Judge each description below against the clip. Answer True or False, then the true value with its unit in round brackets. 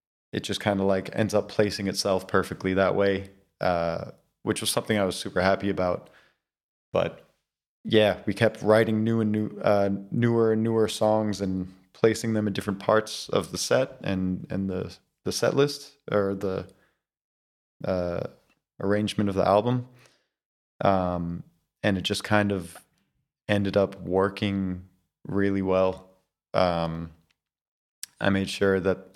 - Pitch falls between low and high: False (100 Hz)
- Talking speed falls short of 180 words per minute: True (150 wpm)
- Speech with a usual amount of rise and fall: False (2.3 semitones)